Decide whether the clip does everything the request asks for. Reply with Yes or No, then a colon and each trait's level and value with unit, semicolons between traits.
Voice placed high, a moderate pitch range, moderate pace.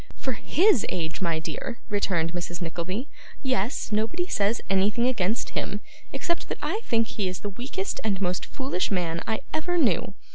No: high, 205 Hz; wide, 5.9 semitones; average, 170 wpm